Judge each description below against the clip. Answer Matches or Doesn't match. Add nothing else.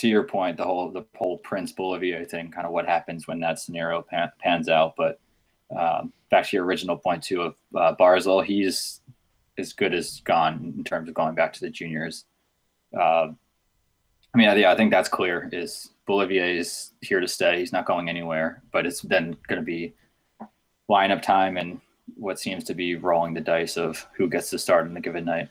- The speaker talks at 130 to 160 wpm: Doesn't match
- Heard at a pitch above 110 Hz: Doesn't match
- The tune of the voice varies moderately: Doesn't match